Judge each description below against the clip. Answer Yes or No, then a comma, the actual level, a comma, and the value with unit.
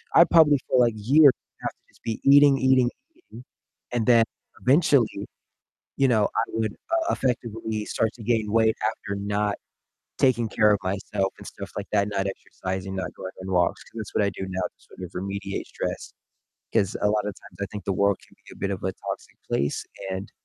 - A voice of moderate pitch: No, low, 105 Hz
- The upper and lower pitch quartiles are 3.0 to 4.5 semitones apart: Yes, average, 3.7 semitones